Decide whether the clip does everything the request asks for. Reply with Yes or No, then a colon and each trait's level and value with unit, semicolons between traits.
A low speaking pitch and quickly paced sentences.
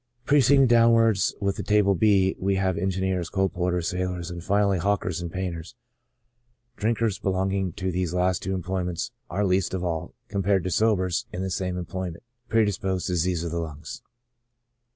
No: very low, 95 Hz; average, 165 wpm